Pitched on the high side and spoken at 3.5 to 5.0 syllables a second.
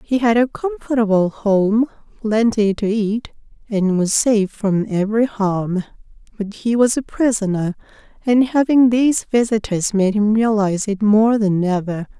Yes: high, 215 Hz; 4.5 syllables/s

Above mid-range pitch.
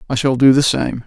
No: low, 130 Hz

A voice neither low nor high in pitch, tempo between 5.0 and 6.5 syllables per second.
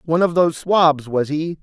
Yes: medium, 160 Hz; 5.3 syllables/s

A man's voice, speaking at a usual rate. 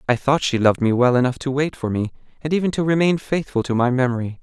No: male; fast, 260 wpm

